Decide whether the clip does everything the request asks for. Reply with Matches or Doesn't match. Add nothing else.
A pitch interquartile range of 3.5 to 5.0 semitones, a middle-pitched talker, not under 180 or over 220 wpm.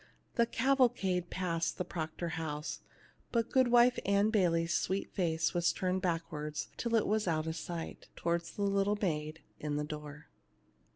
Doesn't match